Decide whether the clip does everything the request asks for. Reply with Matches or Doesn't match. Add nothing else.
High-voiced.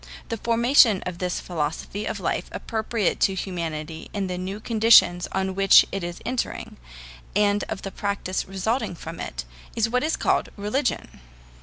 Matches